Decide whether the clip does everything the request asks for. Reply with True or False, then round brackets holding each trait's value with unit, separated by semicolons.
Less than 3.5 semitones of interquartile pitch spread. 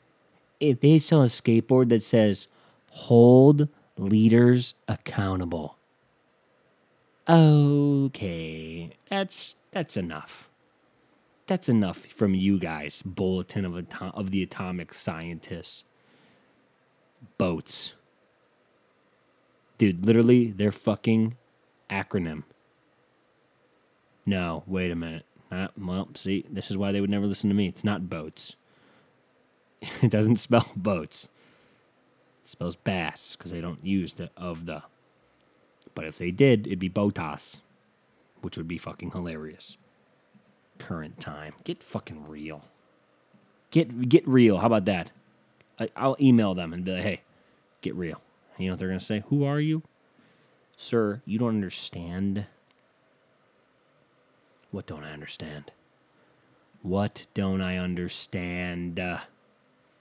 False (4.9 semitones)